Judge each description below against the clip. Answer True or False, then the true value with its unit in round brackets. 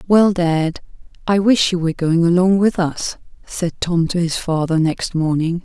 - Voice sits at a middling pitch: True (175 Hz)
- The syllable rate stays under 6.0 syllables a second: True (4.5 syllables/s)